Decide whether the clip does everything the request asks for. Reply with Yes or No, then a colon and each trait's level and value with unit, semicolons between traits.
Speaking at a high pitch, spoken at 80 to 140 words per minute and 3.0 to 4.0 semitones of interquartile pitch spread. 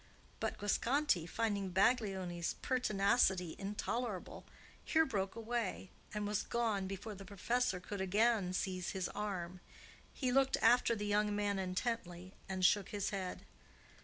Yes: high, 205 Hz; slow, 135 wpm; average, 3.5 semitones